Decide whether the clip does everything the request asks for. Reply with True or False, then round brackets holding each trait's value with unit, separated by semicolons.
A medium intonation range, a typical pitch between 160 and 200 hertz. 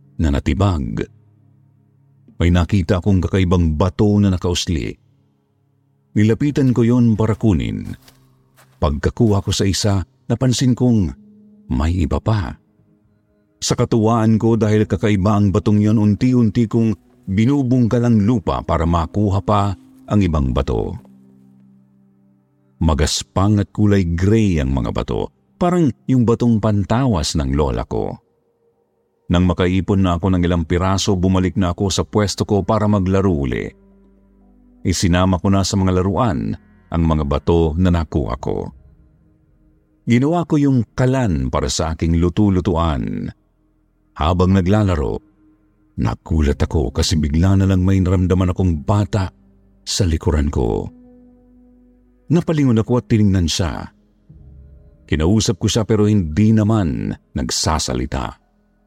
False (4.7 semitones; 100 Hz)